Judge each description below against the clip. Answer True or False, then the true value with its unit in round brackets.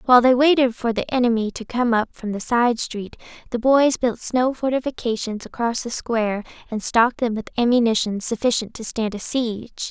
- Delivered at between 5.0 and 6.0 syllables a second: True (5.3 syllables/s)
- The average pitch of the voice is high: True (235 Hz)